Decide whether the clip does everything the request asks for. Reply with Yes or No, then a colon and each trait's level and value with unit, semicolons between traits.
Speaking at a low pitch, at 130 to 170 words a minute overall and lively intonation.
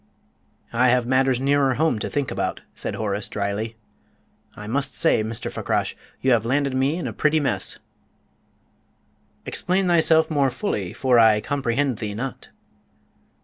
No: low, 130 Hz; average, 145 wpm; average, 4.3 semitones